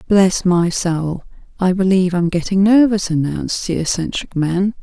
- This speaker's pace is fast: No, average, 150 wpm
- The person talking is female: Yes, female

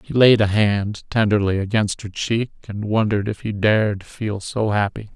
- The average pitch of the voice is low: Yes, low, 105 Hz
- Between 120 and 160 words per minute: No, average, 185 wpm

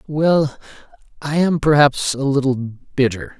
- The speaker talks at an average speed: No, slow, 125 wpm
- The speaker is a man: Yes, male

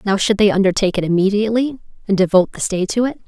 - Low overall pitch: No, high, 200 Hz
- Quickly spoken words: Yes, fast, 220 wpm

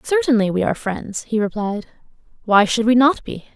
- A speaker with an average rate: Yes, average, 185 wpm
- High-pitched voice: Yes, high, 225 Hz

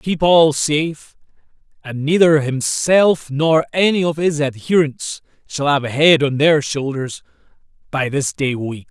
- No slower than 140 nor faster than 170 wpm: Yes, average, 150 wpm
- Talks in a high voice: No, medium, 145 Hz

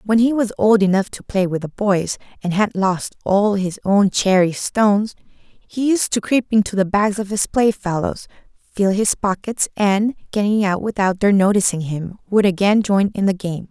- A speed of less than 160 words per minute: No, average, 195 wpm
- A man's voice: No, female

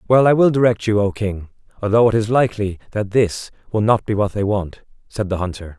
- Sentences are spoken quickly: Yes, fast, 230 wpm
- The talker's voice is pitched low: Yes, low, 105 Hz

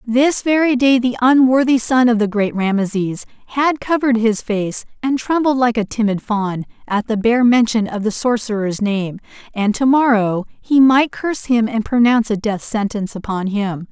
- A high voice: Yes, high, 230 Hz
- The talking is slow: No, average, 180 wpm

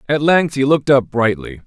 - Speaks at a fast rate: Yes, fast, 215 wpm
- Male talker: Yes, male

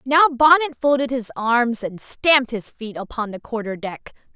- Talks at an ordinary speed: Yes, average, 180 wpm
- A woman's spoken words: Yes, female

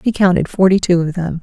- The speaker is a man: No, female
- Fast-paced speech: Yes, fast, 250 wpm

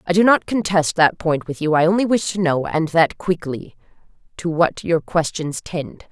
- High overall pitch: No, medium, 170 Hz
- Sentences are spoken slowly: No, fast, 205 wpm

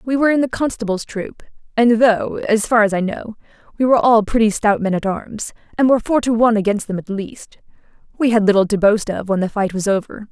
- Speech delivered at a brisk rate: Yes, fast, 240 wpm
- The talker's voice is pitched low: No, high, 220 Hz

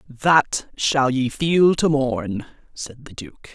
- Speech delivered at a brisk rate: No, average, 150 wpm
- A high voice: No, low, 135 Hz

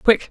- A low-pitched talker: No, high, 220 Hz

